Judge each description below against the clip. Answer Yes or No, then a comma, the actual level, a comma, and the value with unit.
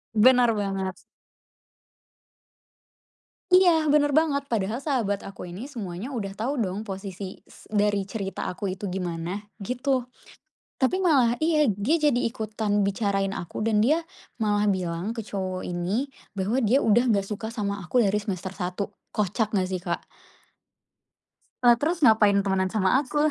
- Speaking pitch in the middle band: No, high, 210 Hz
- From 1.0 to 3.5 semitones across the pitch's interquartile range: No, average, 4.4 semitones